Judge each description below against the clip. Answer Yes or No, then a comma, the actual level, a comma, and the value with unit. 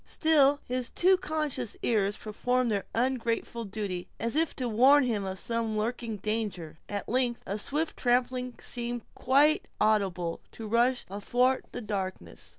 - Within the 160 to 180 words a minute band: No, average, 150 wpm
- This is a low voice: No, high, 235 Hz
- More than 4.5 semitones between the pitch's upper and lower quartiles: No, average, 3.5 semitones